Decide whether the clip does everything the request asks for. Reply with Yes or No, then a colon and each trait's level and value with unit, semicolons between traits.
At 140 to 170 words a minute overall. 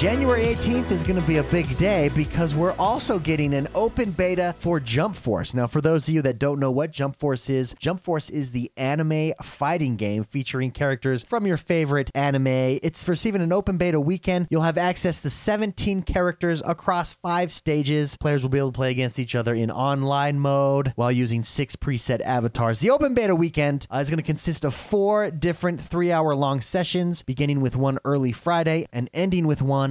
No: average, 200 wpm